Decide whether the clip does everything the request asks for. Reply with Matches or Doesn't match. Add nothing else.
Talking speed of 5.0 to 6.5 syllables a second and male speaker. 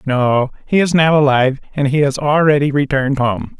Matches